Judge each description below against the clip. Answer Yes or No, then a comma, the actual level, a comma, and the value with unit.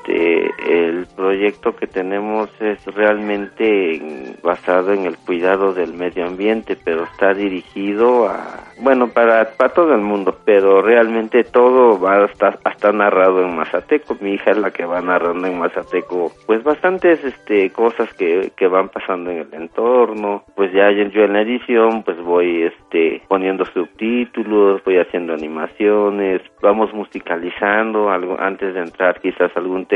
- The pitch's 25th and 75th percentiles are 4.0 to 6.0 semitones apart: No, average, 3.5 semitones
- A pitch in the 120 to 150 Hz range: No, low, 100 Hz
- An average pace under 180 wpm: Yes, average, 155 wpm